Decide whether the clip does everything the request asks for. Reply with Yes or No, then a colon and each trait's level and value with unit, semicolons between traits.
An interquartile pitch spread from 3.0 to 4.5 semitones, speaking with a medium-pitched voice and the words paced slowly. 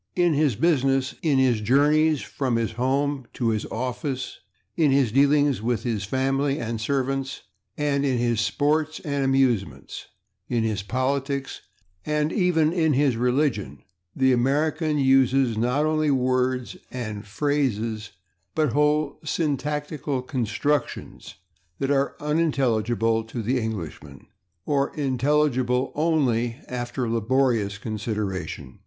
No: average, 3.9 semitones; low, 130 Hz; slow, 120 wpm